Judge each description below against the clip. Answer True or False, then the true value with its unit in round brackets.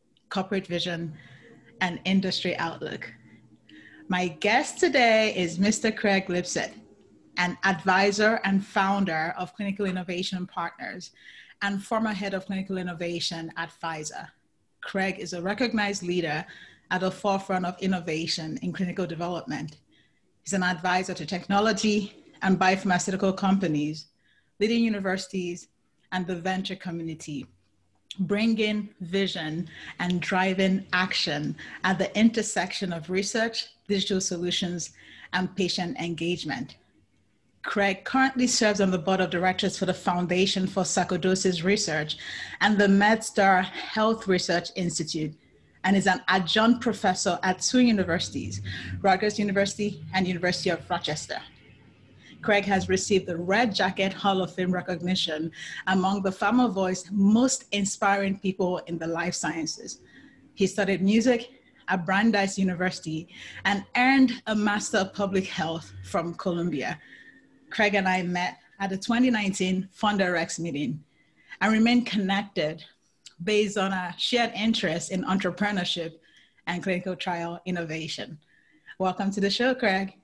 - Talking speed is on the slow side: True (125 wpm)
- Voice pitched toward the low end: False (190 Hz)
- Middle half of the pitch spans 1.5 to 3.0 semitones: True (2.4 semitones)